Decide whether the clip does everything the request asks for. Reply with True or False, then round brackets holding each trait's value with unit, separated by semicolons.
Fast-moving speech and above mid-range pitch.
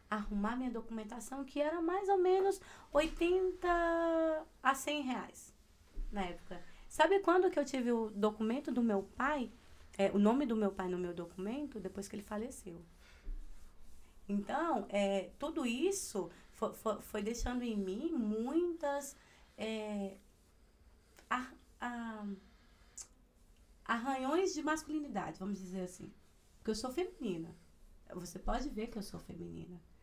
False (135 wpm; 220 Hz)